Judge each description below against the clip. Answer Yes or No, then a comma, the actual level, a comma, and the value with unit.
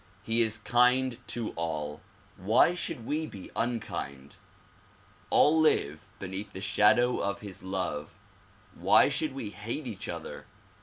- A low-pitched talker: Yes, low, 105 Hz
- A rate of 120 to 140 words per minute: Yes, slow, 135 wpm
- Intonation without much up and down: No, average, 4.8 semitones